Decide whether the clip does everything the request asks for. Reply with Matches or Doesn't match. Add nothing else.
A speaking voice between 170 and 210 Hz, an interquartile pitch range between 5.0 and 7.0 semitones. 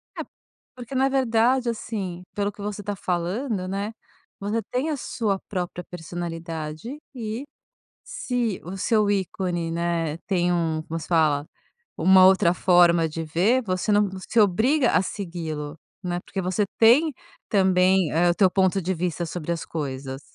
Doesn't match